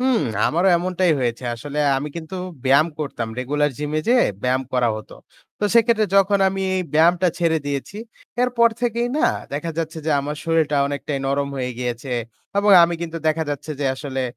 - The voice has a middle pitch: Yes, medium, 155 Hz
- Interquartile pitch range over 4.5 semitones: Yes, average, 5.0 semitones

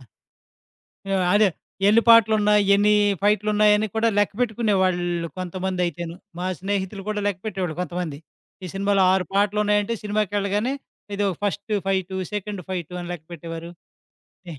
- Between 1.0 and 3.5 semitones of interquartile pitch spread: Yes, narrow, 2.5 semitones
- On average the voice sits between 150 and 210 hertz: Yes, high, 200 Hz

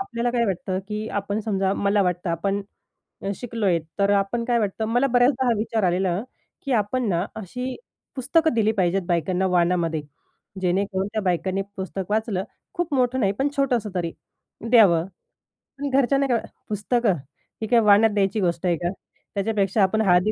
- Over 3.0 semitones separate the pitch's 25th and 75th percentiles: Yes, average, 4.1 semitones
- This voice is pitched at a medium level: No, high, 205 Hz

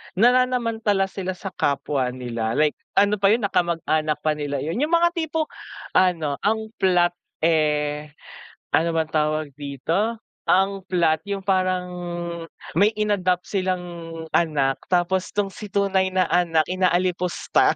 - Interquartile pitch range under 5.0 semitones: Yes, average, 4.3 semitones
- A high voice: No, medium, 180 Hz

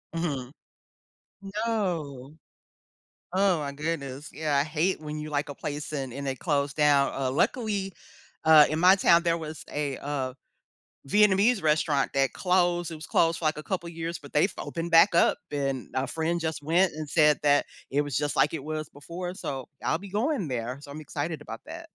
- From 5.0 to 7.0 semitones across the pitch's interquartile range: No, average, 3.3 semitones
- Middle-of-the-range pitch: Yes, medium, 155 Hz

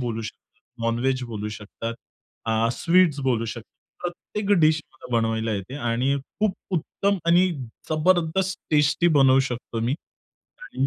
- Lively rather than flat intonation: Yes, wide, 6.6 semitones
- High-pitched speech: No, low, 135 Hz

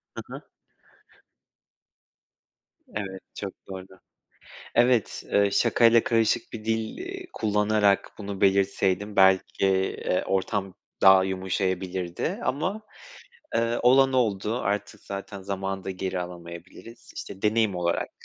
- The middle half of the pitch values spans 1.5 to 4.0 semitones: Yes, average, 3.0 semitones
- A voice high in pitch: No, low, 100 Hz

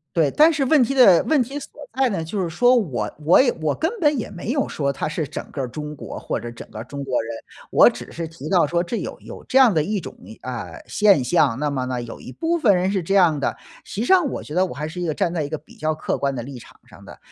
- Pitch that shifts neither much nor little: No, wide, 8.3 semitones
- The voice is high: No, medium, 170 Hz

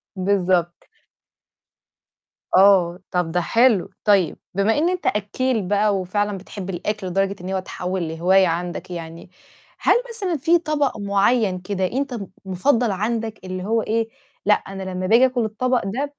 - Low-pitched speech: No, high, 200 Hz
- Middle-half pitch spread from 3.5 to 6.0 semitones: Yes, average, 3.8 semitones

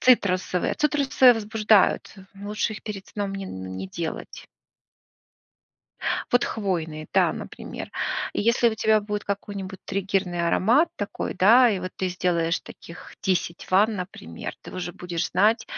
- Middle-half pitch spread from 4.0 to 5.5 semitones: No, average, 3.4 semitones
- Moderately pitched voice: No, high, 195 Hz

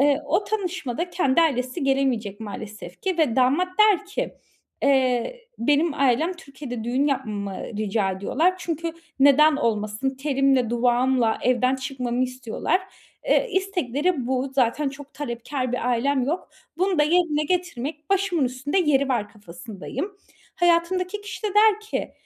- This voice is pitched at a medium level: No, very high, 275 Hz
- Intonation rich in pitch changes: Yes, wide, 5.8 semitones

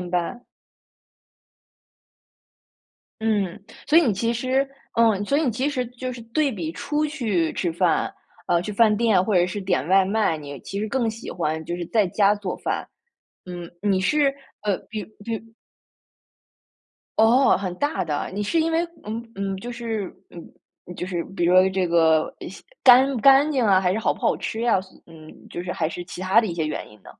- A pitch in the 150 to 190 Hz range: No, high, 205 Hz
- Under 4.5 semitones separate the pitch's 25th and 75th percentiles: No, average, 5.0 semitones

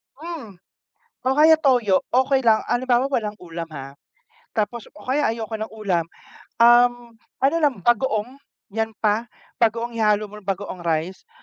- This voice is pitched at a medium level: No, high, 225 Hz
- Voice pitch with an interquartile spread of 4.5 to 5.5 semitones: No, average, 3.8 semitones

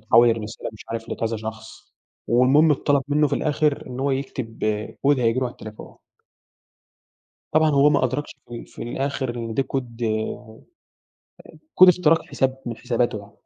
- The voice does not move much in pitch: No, average, 3.7 semitones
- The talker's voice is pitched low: Yes, low, 125 Hz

